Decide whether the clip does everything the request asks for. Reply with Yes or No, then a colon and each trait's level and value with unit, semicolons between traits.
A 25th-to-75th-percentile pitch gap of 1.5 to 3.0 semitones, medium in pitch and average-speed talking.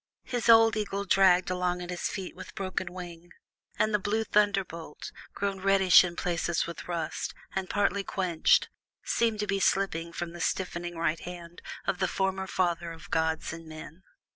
Yes: narrow, 2.5 semitones; medium, 180 Hz; average, 170 wpm